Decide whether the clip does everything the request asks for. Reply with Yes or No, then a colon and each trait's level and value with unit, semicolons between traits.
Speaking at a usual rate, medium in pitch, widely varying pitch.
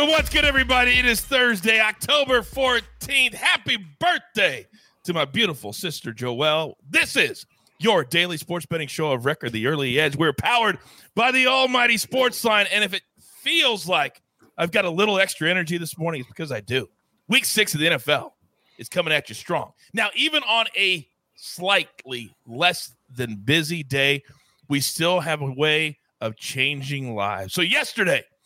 Yes: average, 170 wpm; medium, 170 Hz; wide, 8.1 semitones